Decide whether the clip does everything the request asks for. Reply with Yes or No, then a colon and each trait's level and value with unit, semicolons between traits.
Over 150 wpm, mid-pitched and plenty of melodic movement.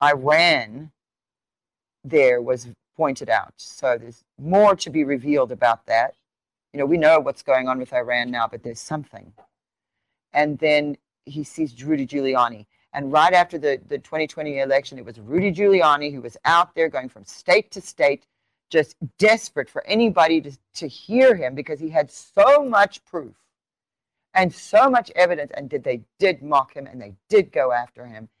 Yes: average, 175 wpm; medium, 150 Hz; wide, 5.9 semitones